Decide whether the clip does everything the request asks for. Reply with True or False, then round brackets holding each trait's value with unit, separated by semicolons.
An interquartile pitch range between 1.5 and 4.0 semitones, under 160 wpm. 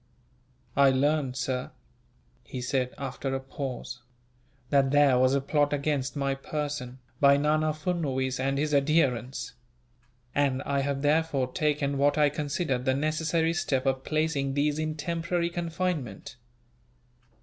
True (2.5 semitones; 135 wpm)